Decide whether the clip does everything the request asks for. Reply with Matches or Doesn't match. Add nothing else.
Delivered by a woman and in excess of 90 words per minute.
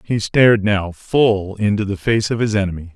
Doesn't match